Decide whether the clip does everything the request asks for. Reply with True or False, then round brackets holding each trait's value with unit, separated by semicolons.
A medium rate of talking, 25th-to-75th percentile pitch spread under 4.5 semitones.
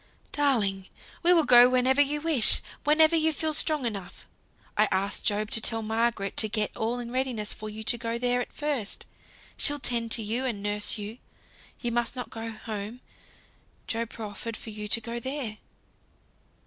True (175 wpm; 3.4 semitones)